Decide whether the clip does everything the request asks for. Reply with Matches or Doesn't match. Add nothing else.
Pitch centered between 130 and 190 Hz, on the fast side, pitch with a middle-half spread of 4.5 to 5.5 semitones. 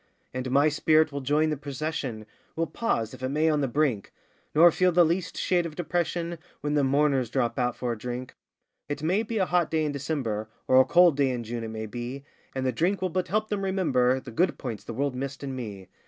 Matches